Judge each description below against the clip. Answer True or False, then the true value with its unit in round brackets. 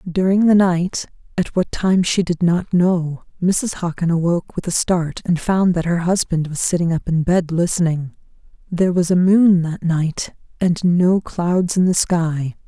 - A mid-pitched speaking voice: True (175 Hz)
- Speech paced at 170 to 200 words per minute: True (185 wpm)